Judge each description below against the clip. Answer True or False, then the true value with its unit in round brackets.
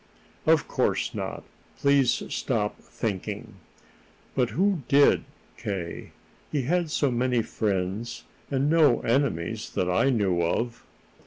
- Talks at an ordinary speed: False (115 wpm)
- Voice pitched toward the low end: True (120 Hz)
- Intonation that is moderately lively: False (5.7 semitones)